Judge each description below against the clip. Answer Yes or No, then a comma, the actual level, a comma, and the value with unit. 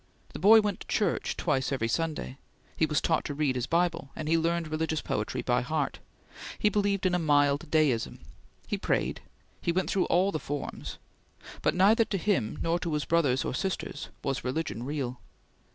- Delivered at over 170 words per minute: Yes, average, 185 wpm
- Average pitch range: Yes, average, 4.0 semitones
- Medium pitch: Yes, medium, 160 Hz